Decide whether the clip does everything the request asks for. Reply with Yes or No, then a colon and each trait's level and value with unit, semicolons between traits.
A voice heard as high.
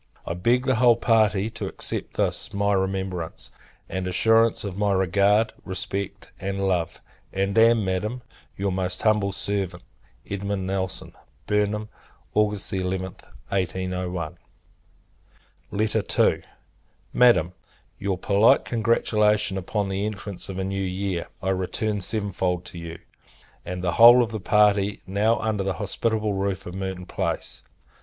No: low, 100 Hz